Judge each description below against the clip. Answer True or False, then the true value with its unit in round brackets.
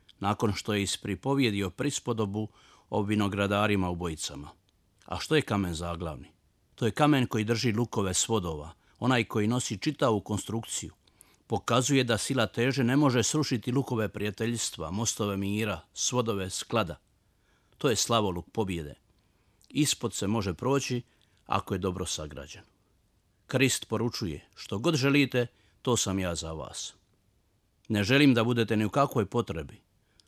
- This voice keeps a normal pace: True (140 wpm)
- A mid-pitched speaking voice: False (105 Hz)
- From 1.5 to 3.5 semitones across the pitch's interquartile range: False (4.2 semitones)